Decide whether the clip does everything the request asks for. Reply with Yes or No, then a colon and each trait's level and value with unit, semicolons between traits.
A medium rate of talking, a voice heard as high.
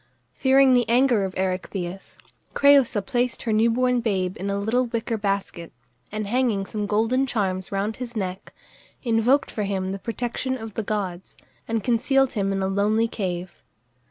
Yes: average, 165 wpm; high, 215 Hz